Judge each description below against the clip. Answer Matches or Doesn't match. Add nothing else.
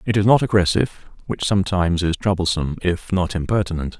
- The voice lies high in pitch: Doesn't match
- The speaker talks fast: Doesn't match